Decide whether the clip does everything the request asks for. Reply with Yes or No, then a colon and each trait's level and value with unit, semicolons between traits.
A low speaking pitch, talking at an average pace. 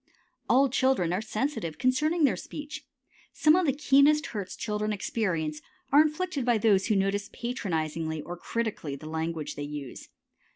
No: high, 210 Hz; average, 155 wpm